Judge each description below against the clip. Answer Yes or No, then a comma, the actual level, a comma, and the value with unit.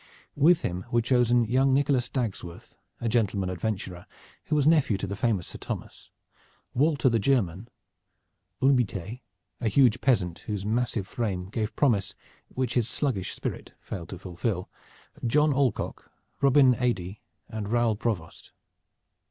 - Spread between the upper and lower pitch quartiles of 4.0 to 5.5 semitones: Yes, average, 4.9 semitones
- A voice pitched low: Yes, low, 115 Hz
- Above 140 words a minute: No, slow, 135 wpm